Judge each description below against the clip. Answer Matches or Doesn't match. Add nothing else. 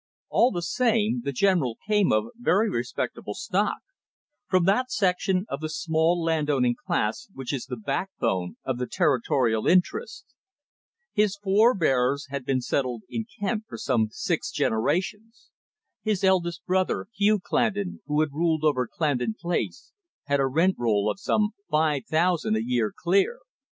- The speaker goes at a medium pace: Matches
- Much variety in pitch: Matches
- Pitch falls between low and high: Matches